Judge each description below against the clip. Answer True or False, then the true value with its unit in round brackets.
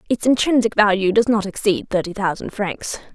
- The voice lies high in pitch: True (205 Hz)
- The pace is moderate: True (170 wpm)